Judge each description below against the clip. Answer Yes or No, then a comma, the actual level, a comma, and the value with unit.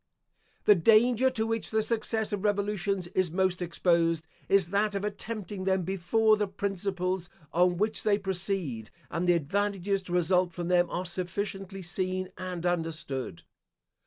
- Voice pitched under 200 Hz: Yes, high, 190 Hz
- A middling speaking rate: Yes, average, 150 wpm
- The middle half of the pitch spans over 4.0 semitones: No, narrow, 2.6 semitones